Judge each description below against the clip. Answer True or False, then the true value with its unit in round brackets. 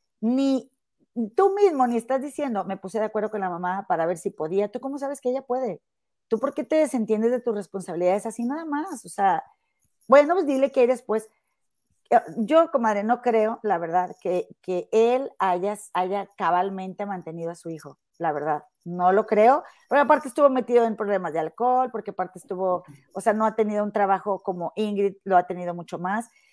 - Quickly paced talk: True (200 wpm)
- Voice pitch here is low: False (215 Hz)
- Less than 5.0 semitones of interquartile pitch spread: False (5.6 semitones)